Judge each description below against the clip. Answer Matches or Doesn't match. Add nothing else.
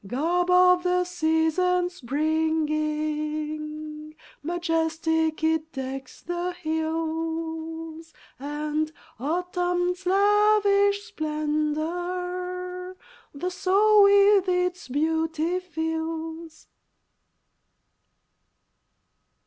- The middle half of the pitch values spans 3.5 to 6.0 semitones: Doesn't match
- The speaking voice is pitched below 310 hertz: Doesn't match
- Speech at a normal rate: Doesn't match